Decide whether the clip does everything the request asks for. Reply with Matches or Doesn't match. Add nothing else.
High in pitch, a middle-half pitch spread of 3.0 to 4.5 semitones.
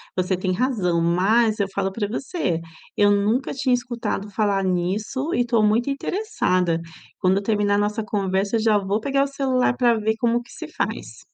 Matches